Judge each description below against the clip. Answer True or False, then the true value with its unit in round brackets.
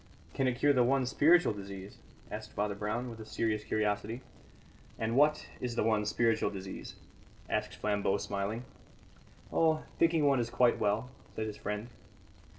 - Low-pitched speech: True (110 Hz)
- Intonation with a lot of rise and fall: False (3.4 semitones)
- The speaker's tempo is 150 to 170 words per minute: True (155 wpm)